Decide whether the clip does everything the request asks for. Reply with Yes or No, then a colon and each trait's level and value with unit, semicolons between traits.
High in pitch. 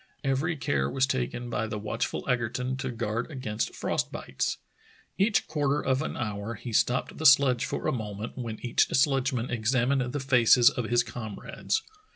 No: low, 125 Hz